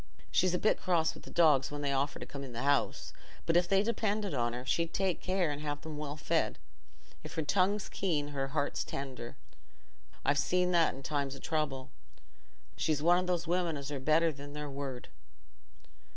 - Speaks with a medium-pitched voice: Yes, medium, 150 Hz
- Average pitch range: Yes, average, 3.9 semitones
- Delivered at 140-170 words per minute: No, average, 200 wpm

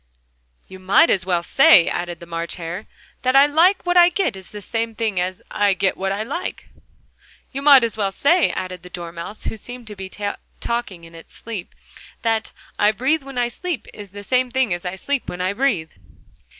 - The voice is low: No, high, 210 Hz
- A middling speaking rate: No, fast, 215 wpm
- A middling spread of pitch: No, wide, 6.2 semitones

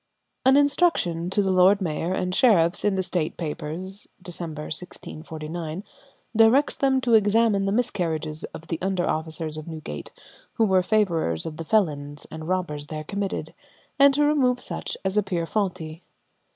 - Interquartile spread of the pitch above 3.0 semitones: Yes, average, 4.7 semitones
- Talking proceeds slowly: No, average, 155 wpm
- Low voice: No, medium, 180 Hz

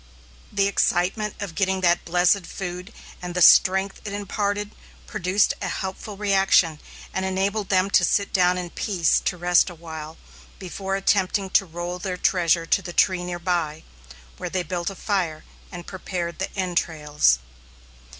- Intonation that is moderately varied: No, narrow, 2.0 semitones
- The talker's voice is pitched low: No, medium, 185 Hz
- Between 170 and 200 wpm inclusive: No, average, 160 wpm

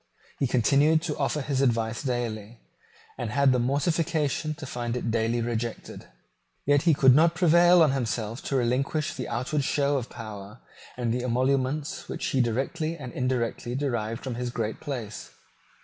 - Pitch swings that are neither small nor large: Yes, average, 3.6 semitones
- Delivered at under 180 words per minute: Yes, average, 165 wpm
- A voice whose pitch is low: Yes, low, 130 Hz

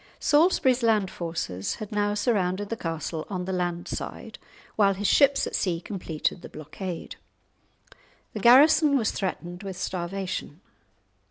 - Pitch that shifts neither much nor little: Yes, average, 3.9 semitones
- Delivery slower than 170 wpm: Yes, average, 140 wpm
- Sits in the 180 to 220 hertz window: Yes, high, 190 Hz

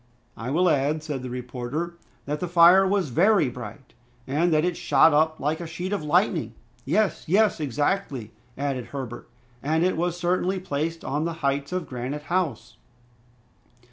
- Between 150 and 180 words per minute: Yes, average, 165 wpm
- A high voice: No, medium, 155 Hz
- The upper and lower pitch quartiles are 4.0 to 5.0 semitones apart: Yes, average, 4.4 semitones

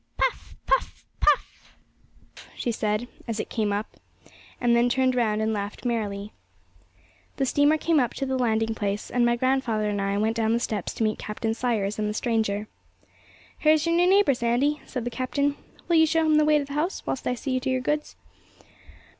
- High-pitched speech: Yes, high, 240 Hz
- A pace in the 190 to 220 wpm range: Yes, average, 195 wpm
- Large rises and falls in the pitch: No, average, 4.5 semitones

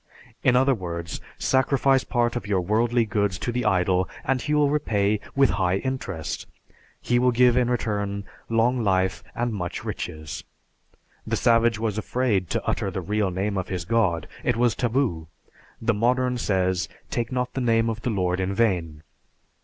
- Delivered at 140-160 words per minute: No, average, 170 wpm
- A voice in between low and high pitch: No, low, 110 Hz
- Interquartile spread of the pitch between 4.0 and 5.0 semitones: Yes, average, 4.6 semitones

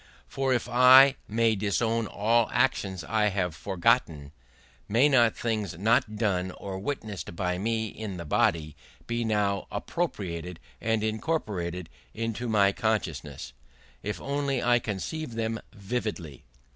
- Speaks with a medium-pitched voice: No, low, 105 Hz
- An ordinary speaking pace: No, slow, 130 wpm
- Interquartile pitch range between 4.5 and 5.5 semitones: No, average, 3.9 semitones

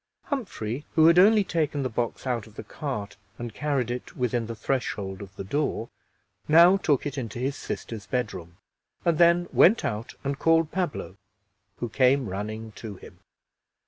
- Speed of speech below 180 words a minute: Yes, average, 170 wpm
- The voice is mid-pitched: No, low, 125 Hz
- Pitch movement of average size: No, wide, 6.1 semitones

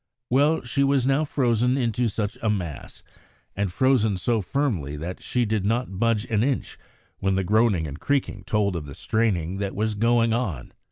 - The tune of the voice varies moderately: Yes, average, 4.3 semitones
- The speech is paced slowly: No, average, 180 wpm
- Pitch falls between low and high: No, low, 110 Hz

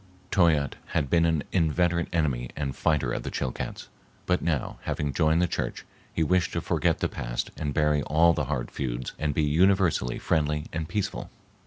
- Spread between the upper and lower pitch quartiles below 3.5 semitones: Yes, average, 3.1 semitones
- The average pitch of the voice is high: No, very low, 75 Hz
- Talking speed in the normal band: Yes, average, 180 wpm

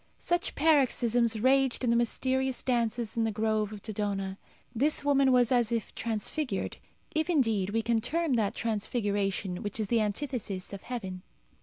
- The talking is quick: No, average, 160 wpm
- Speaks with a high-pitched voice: Yes, high, 230 Hz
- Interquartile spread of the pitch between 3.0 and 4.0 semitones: Yes, average, 3.7 semitones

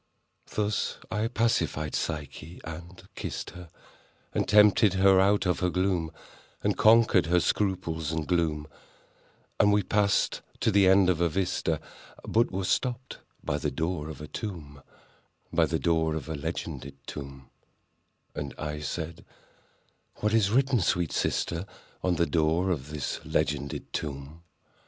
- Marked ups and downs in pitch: No, average, 4.3 semitones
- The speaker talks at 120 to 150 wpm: Yes, average, 140 wpm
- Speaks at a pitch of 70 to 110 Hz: Yes, very low, 85 Hz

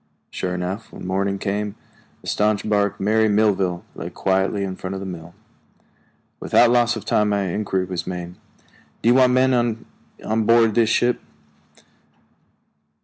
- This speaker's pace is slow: No, average, 155 wpm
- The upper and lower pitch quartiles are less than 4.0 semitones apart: Yes, average, 3.0 semitones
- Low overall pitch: Yes, low, 105 Hz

